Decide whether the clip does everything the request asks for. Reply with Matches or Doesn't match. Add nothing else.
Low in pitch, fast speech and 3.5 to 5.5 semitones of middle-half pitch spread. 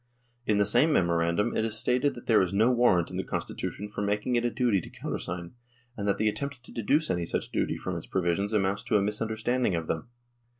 Matches